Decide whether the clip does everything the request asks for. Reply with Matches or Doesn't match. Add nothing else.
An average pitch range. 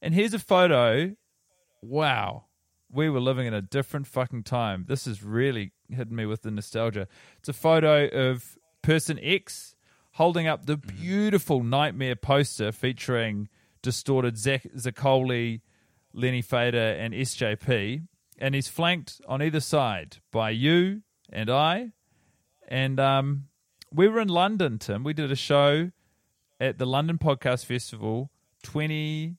Matches